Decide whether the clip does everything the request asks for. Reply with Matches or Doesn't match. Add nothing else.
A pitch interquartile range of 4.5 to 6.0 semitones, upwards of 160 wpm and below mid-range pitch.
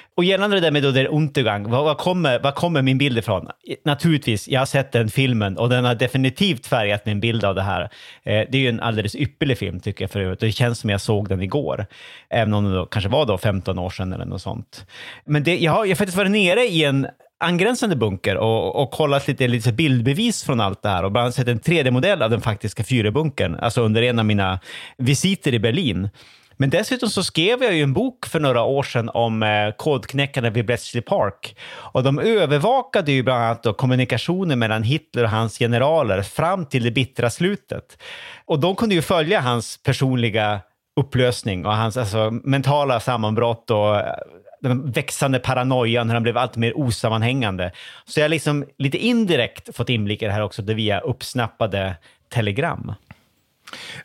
Matches